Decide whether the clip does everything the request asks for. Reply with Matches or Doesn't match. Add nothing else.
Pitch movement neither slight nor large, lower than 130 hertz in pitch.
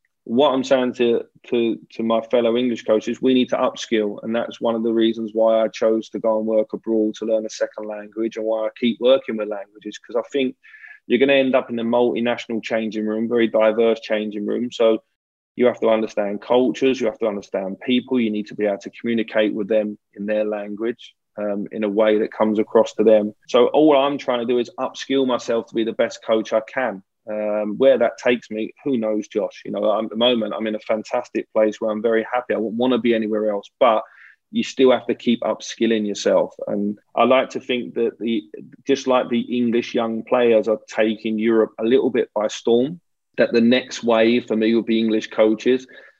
Doesn't match